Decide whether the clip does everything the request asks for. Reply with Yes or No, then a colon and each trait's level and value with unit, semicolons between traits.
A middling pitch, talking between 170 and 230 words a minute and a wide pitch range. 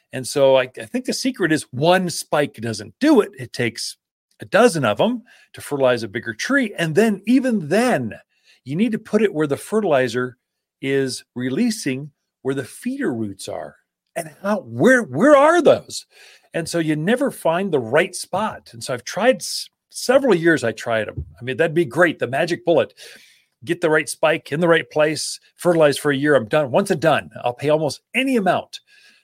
Yes: medium, 165 Hz; average, 195 wpm; wide, 9.0 semitones